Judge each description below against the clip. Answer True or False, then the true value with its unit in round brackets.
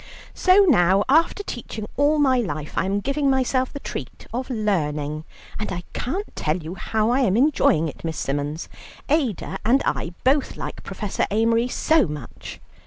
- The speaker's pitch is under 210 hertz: False (225 Hz)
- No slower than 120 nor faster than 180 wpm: True (170 wpm)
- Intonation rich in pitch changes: True (7.9 semitones)